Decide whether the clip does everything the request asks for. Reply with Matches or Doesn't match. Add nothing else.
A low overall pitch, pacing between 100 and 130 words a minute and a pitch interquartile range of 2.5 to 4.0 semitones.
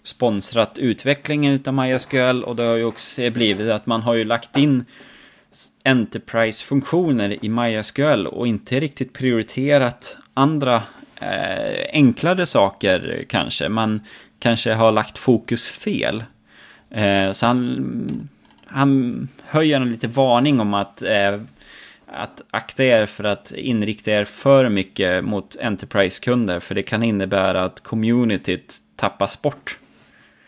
Matches